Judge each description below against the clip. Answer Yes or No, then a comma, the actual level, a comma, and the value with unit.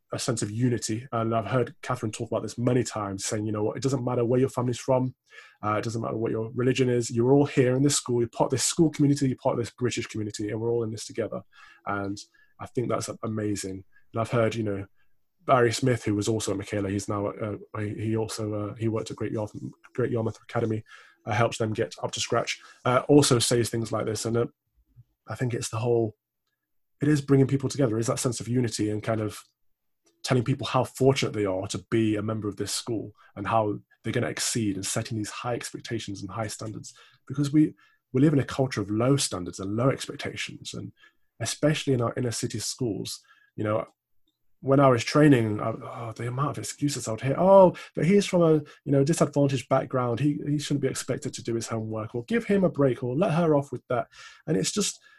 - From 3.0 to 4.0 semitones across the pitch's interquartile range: Yes, average, 3.7 semitones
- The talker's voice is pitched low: Yes, low, 120 Hz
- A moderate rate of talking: No, fast, 230 wpm